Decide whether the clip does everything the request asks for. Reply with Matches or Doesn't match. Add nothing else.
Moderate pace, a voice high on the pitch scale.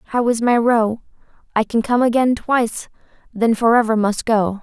Matches